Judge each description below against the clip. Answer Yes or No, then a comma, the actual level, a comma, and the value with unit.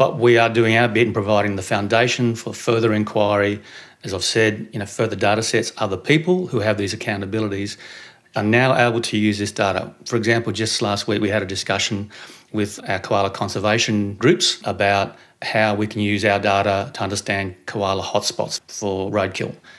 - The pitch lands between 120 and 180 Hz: No, low, 105 Hz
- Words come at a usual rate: Yes, average, 190 wpm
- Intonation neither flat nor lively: No, narrow, 2.3 semitones